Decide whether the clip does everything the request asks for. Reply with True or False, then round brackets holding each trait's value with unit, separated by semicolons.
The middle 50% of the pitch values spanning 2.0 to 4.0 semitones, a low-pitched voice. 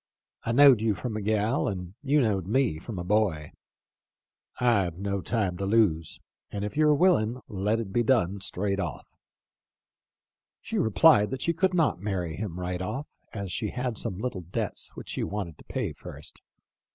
False (4.6 semitones; 105 Hz)